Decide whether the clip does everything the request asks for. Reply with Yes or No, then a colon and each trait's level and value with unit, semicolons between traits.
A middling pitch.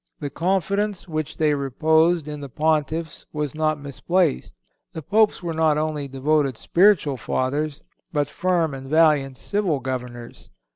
Yes: medium, 155 Hz